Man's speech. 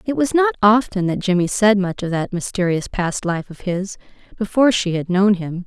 No: female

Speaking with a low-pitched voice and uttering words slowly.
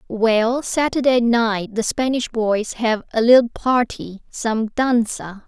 No: high, 230 Hz; slow, 130 wpm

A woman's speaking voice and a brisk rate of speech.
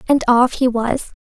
No: female; average, 195 wpm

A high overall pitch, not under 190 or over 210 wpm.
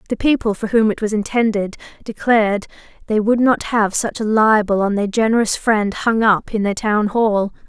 Yes: high, 215 Hz; average, 195 wpm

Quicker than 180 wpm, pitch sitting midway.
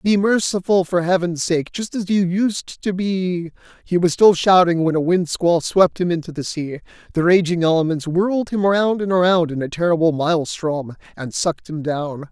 Yes: average, 190 wpm; medium, 175 Hz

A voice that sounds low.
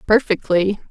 No: high, 200 Hz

